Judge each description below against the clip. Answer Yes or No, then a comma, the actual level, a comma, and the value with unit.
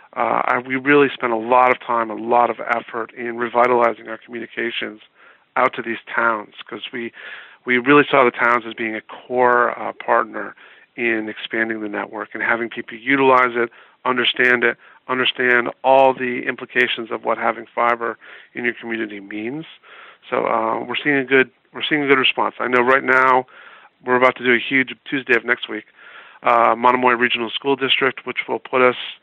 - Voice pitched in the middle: No, low, 120 Hz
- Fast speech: No, average, 190 wpm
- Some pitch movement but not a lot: No, narrow, 1.8 semitones